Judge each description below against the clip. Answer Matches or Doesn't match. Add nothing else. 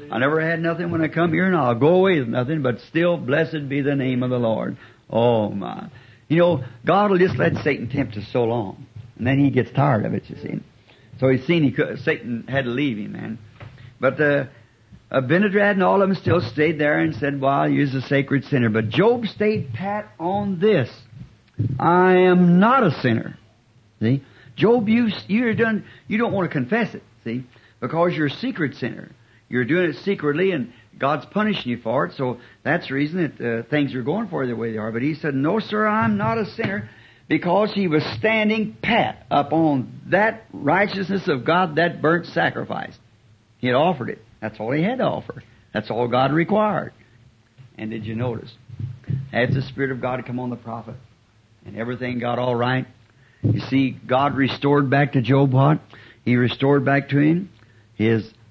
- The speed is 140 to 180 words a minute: Doesn't match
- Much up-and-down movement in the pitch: Matches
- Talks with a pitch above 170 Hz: Doesn't match